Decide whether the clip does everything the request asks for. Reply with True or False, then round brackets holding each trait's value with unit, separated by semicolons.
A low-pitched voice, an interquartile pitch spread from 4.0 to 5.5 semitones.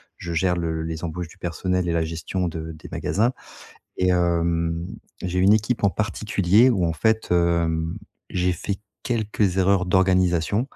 False (90 Hz; 2.8 semitones)